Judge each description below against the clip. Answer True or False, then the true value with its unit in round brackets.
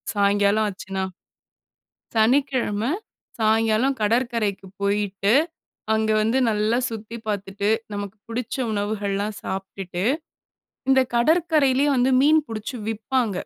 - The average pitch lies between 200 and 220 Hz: True (215 Hz)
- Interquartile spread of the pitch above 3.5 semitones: False (3.2 semitones)